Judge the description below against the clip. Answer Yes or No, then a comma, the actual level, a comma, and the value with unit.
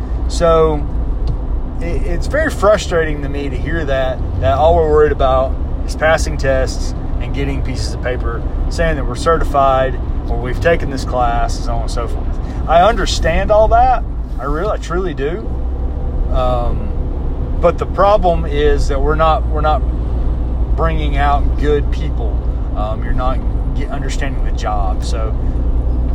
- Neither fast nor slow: Yes, average, 160 wpm